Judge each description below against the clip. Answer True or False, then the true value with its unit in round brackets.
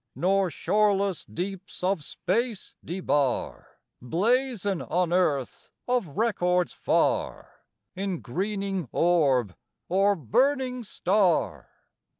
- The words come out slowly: True (90 wpm)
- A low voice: False (190 Hz)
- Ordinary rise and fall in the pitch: True (3.5 semitones)